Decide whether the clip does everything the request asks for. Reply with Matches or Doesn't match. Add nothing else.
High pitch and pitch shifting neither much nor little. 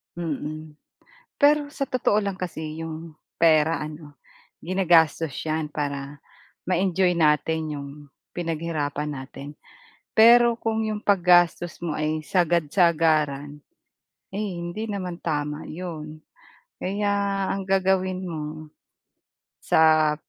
Doesn't match